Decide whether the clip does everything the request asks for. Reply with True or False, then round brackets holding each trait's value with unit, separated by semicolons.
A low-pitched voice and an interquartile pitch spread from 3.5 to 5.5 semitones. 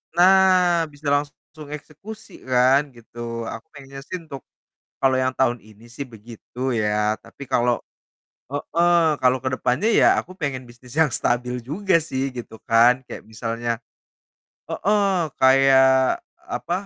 True (130 Hz; 4.4 semitones)